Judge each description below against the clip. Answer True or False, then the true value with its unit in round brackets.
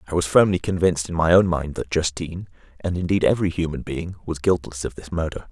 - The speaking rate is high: True (220 wpm)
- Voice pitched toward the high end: False (85 Hz)